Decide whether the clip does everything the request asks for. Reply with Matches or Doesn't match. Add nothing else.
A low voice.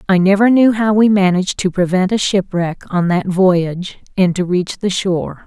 Doesn't match